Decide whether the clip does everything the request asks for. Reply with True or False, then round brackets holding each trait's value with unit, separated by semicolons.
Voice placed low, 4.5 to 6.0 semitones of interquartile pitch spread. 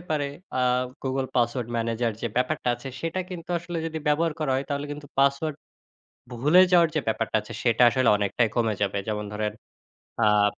True (130 Hz; 5.0 semitones)